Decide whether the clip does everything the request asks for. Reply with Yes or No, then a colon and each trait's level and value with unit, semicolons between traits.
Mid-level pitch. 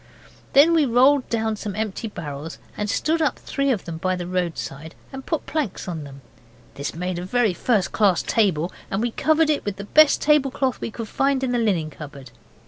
No: high, 215 Hz